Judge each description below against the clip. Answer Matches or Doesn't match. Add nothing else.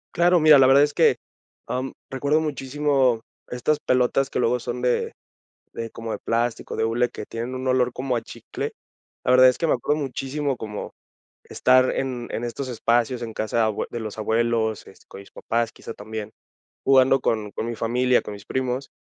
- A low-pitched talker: Matches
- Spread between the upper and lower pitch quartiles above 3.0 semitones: Doesn't match